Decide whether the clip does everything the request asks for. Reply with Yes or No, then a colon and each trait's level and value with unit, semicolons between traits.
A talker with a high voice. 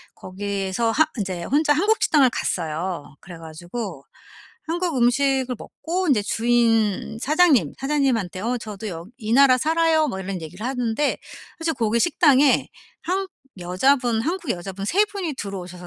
Yes: high, 235 Hz